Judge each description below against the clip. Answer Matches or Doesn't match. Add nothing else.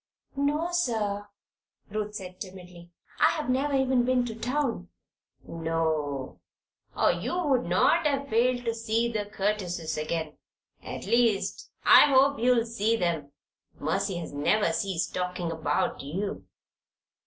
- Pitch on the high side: Matches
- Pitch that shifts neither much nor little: Doesn't match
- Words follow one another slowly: Matches